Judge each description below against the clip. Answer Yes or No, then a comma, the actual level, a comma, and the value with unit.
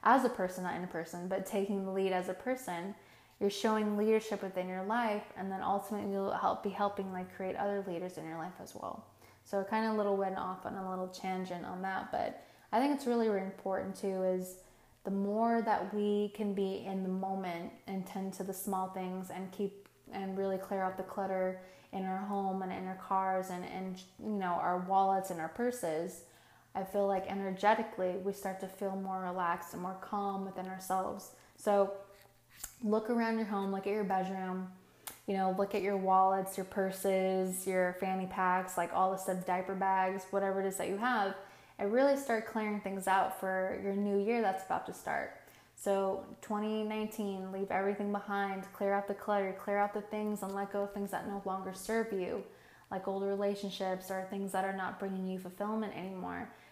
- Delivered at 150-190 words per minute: No, fast, 205 wpm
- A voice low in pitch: No, high, 195 Hz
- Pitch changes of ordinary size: No, narrow, 1.3 semitones